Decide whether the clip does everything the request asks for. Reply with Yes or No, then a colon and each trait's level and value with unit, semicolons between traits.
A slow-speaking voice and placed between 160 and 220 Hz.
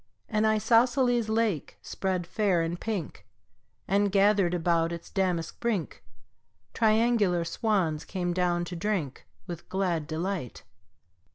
Yes: slow, 115 wpm; high, 190 Hz